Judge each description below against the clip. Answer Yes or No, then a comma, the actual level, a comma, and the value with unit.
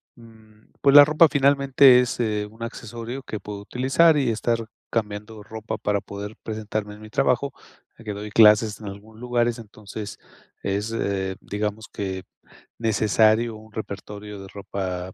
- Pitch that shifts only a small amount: Yes, narrow, 2.3 semitones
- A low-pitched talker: Yes, low, 110 Hz